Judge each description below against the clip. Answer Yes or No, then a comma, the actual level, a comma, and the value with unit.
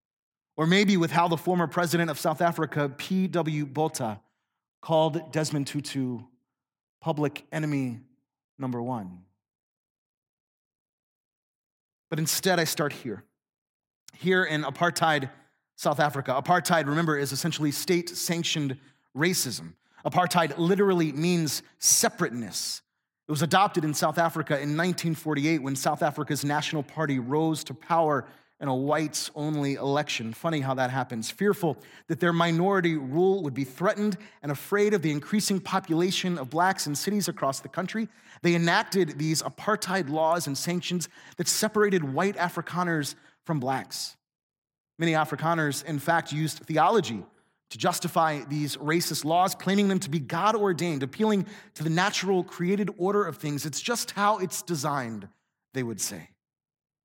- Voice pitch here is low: No, medium, 160 Hz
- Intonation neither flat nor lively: Yes, average, 3.5 semitones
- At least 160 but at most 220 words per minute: No, average, 140 wpm